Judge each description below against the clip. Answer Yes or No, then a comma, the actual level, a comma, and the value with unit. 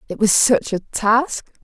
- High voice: Yes, high, 225 Hz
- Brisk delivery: No, average, 185 wpm